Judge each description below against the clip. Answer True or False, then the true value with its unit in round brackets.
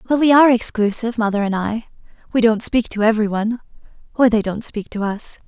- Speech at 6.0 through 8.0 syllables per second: True (6.1 syllables/s)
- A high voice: True (225 Hz)